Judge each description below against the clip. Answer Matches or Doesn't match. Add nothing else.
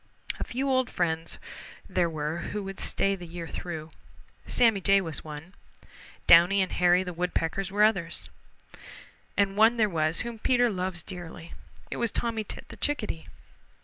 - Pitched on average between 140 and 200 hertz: Matches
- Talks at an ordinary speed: Matches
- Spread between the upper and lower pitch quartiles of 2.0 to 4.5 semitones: Matches